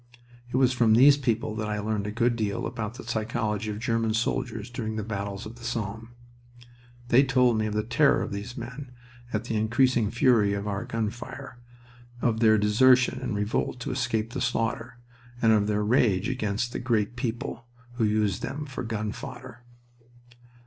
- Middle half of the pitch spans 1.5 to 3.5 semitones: Yes, narrow, 2.5 semitones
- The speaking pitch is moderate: No, low, 115 Hz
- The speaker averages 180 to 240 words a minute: Yes, average, 185 wpm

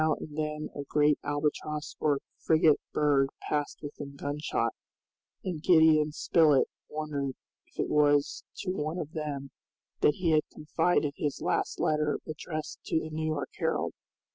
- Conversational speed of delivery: Yes, average, 150 wpm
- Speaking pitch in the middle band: Yes, medium, 150 Hz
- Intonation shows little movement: Yes, narrow, 1.3 semitones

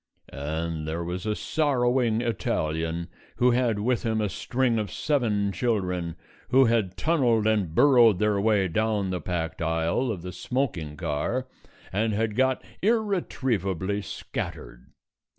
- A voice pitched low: Yes, low, 105 Hz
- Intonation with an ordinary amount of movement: No, wide, 5.7 semitones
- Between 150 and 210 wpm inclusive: No, slow, 135 wpm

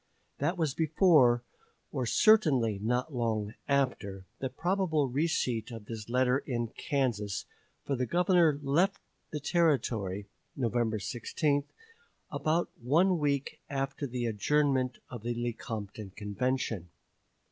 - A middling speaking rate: No, slow, 115 wpm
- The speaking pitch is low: Yes, low, 130 Hz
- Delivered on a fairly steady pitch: No, average, 4.6 semitones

